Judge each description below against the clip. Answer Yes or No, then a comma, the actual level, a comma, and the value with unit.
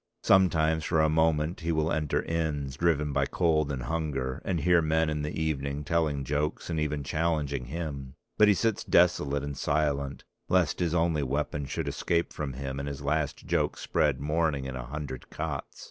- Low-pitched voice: Yes, very low, 75 Hz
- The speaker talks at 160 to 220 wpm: Yes, average, 185 wpm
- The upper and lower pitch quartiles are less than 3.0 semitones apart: Yes, narrow, 2.6 semitones